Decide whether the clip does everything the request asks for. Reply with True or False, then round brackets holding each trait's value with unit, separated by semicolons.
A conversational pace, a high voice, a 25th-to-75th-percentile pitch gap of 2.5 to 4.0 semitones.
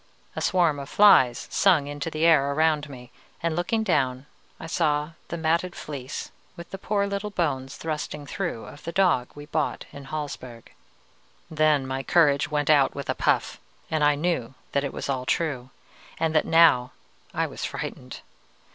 False (175 wpm; 150 Hz; 3.3 semitones)